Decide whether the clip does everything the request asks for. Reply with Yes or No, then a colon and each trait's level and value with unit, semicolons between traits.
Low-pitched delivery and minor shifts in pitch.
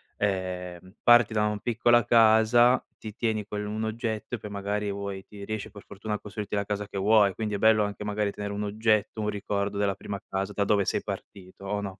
Yes: low, 105 Hz; narrow, 1.4 semitones